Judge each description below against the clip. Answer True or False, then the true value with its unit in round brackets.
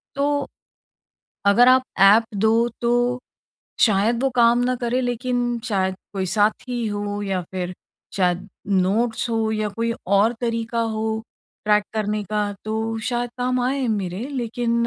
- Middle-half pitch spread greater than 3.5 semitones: False (2.9 semitones)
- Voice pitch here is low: False (225 Hz)